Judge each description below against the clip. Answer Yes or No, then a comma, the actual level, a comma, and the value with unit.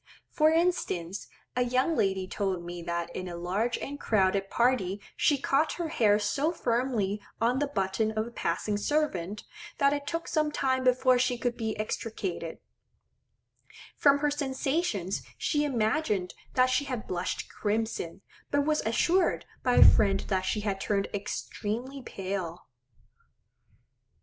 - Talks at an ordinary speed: Yes, average, 145 wpm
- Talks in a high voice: Yes, high, 230 Hz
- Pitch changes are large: Yes, wide, 6.2 semitones